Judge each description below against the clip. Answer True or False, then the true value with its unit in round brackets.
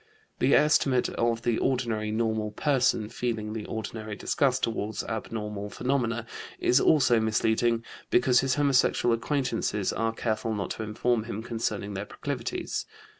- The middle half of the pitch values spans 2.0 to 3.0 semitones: True (2.4 semitones)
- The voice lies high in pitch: False (115 Hz)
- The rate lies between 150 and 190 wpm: False (135 wpm)